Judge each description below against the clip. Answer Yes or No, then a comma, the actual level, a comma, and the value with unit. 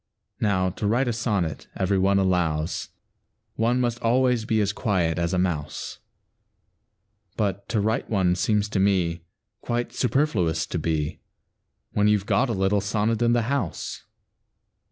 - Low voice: Yes, low, 100 Hz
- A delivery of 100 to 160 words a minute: Yes, average, 155 wpm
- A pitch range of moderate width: Yes, average, 4.3 semitones